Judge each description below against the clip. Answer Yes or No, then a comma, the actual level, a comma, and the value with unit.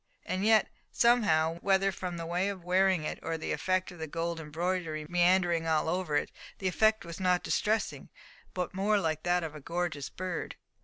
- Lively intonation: No, narrow, 2.5 semitones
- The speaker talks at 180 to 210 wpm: Yes, average, 190 wpm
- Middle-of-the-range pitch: Yes, medium, 175 Hz